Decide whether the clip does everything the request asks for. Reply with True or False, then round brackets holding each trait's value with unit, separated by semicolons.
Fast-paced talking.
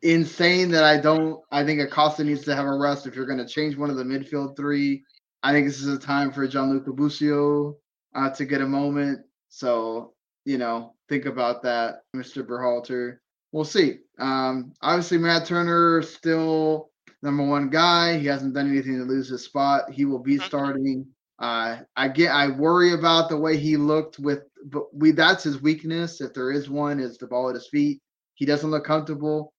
False (195 wpm)